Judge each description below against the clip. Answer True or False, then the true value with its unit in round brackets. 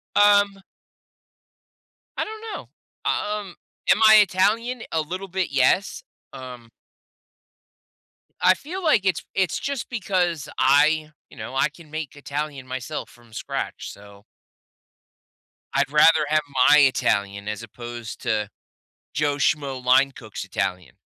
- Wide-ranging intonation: True (7.0 semitones)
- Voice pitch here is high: False (150 Hz)